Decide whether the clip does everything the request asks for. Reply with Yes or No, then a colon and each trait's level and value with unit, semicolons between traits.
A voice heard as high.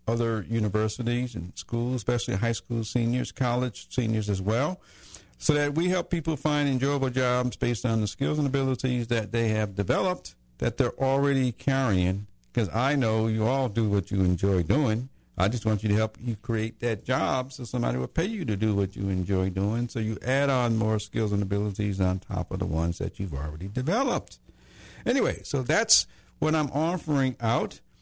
No: low, 115 Hz